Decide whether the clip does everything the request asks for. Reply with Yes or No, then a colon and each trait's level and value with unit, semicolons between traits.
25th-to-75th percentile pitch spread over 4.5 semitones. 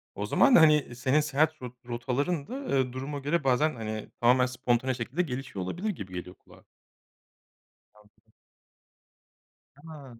No: average, 4.1 semitones